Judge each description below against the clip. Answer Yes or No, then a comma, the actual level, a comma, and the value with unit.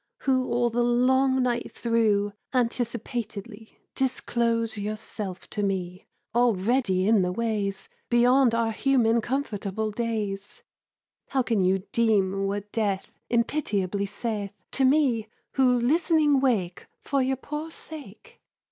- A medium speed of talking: No, slow, 120 wpm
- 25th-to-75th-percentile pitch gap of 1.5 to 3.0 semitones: No, average, 3.9 semitones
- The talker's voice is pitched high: Yes, high, 230 Hz